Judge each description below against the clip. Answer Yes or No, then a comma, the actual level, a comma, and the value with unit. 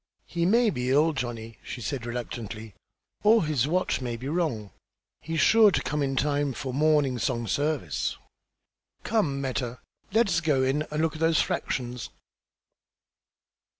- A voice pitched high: No, medium, 140 Hz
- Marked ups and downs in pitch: No, average, 4.5 semitones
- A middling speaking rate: Yes, average, 150 wpm